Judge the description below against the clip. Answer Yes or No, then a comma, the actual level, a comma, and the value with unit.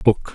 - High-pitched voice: No, low, 105 Hz